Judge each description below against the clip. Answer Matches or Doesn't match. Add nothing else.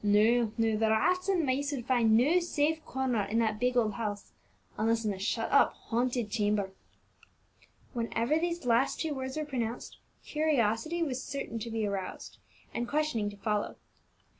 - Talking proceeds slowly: Doesn't match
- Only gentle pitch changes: Doesn't match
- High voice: Matches